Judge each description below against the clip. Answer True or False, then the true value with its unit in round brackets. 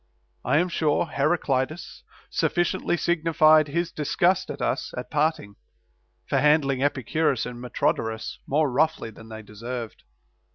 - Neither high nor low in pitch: True (150 Hz)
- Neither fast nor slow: False (125 wpm)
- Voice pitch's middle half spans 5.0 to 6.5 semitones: False (4.4 semitones)